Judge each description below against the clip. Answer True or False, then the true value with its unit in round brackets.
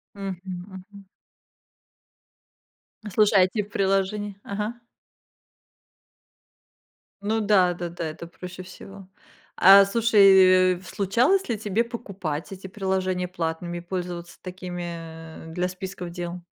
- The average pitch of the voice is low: False (185 Hz)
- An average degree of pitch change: False (2.2 semitones)